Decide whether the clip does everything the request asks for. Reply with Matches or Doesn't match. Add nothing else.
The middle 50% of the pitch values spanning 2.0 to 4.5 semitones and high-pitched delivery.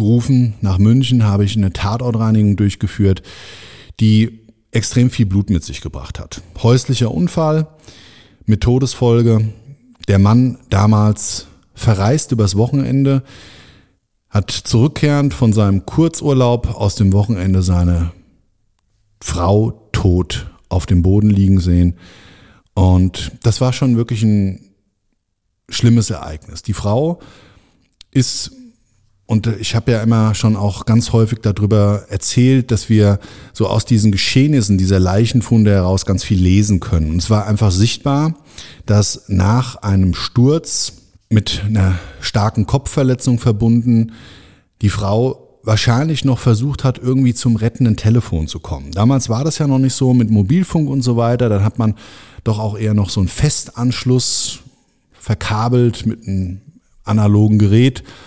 Doesn't match